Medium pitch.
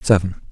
No: very low, 95 Hz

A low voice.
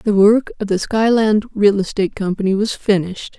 No: high, 205 Hz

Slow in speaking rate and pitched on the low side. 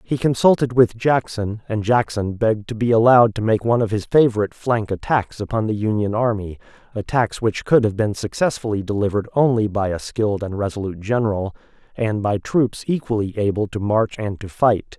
No: average, 185 wpm; low, 110 Hz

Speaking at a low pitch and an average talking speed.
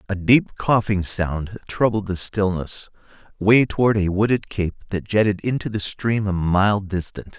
Yes: low, 100 Hz; average, 165 wpm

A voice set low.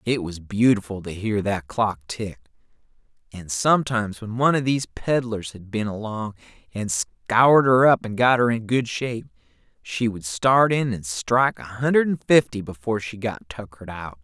Yes: low, 110 Hz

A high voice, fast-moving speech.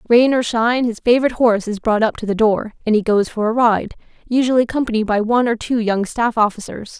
Yes: high, 225 Hz; fast, 230 wpm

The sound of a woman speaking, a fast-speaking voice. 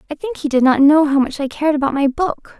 Yes: female; fast, 300 wpm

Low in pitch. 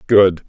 Yes: very low, 95 Hz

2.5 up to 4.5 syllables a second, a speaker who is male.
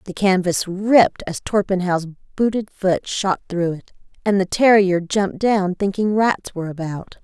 No: 4.3 syllables/s; female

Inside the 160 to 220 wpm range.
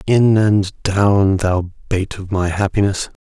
No: average, 150 wpm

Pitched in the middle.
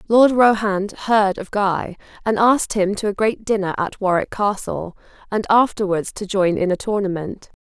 No: high, 200 Hz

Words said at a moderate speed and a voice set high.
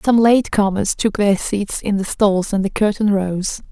Yes: average, 195 wpm; high, 205 Hz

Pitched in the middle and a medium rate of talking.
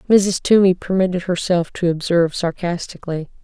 No: medium, 180 Hz; slow, 120 wpm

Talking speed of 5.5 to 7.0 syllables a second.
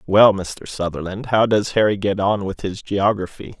No: 4.6 syllables/s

